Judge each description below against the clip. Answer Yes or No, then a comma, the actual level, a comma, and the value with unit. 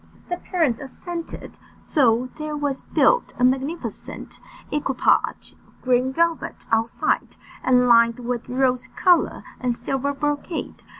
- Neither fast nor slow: No, slow, 120 wpm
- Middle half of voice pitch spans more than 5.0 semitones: No, average, 3.5 semitones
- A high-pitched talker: Yes, very high, 265 Hz